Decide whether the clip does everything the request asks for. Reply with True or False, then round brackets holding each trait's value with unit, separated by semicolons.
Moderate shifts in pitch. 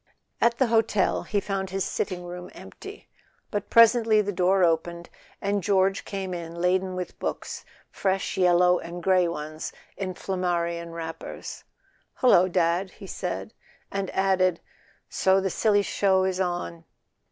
False (2.0 semitones)